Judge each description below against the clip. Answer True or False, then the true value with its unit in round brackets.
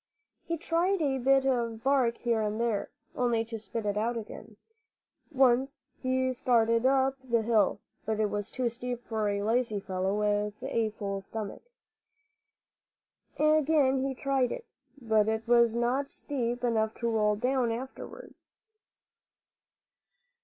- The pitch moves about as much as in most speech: True (3.2 semitones)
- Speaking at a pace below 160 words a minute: True (140 wpm)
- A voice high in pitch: True (235 Hz)